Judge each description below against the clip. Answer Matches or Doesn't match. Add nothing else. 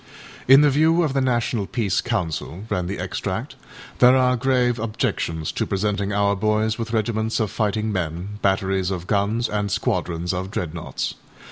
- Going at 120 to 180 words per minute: Matches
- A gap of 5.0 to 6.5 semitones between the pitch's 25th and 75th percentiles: Doesn't match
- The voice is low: Matches